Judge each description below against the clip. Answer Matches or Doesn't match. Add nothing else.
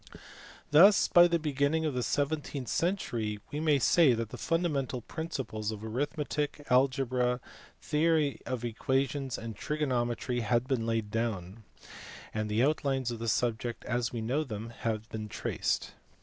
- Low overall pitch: Matches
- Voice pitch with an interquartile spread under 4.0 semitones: Doesn't match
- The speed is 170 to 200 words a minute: Doesn't match